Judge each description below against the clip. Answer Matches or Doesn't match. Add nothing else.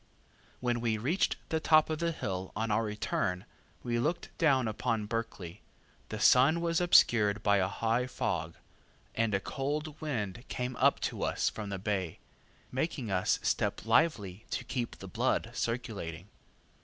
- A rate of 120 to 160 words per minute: Matches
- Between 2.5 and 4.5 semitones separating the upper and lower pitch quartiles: Doesn't match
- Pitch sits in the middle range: Doesn't match